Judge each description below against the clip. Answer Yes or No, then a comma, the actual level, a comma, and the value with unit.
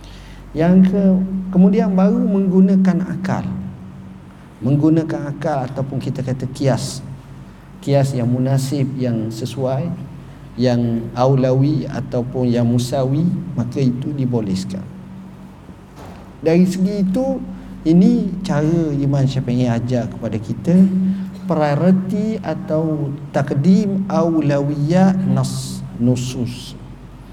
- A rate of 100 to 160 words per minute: No, slow, 90 wpm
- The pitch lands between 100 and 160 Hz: Yes, medium, 140 Hz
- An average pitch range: No, wide, 6.3 semitones